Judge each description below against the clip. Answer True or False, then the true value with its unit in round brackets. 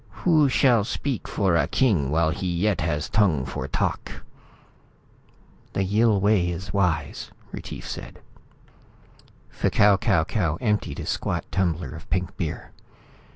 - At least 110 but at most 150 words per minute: True (135 wpm)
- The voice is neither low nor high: False (95 Hz)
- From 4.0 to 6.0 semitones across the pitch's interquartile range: True (4.4 semitones)